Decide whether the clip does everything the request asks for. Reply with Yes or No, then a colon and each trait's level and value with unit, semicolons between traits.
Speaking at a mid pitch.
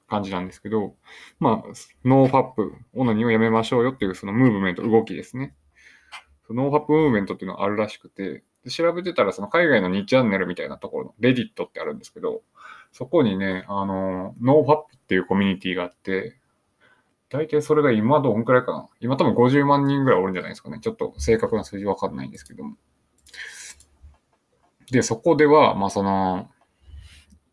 No: low, 110 Hz